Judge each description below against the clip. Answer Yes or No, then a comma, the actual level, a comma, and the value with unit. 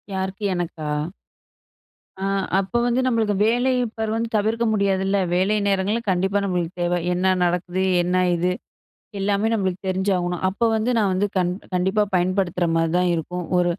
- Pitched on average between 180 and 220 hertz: Yes, high, 190 Hz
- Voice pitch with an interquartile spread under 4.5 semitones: Yes, average, 2.7 semitones